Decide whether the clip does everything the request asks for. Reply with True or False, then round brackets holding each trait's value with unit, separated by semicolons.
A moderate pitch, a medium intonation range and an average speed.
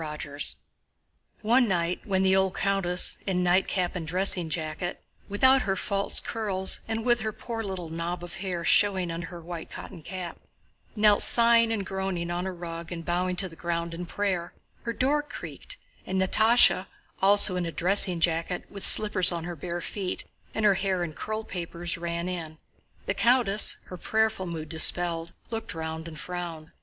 True (180 Hz; 3.0 semitones; 170 wpm)